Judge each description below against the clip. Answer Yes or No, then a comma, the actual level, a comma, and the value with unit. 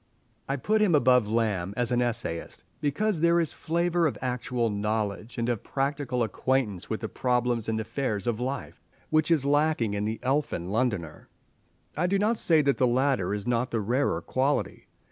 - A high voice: No, low, 125 Hz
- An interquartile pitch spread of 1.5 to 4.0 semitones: No, average, 4.8 semitones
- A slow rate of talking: No, average, 185 wpm